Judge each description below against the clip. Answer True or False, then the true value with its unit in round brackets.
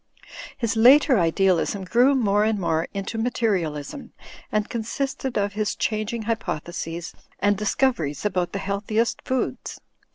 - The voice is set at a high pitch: True (210 Hz)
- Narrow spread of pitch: False (3.8 semitones)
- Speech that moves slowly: True (125 wpm)